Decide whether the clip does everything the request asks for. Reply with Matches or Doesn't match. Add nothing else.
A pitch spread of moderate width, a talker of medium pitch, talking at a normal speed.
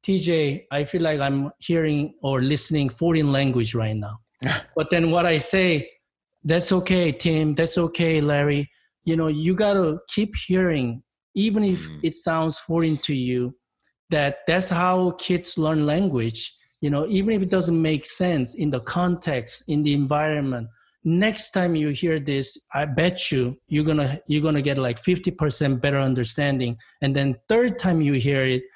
Matches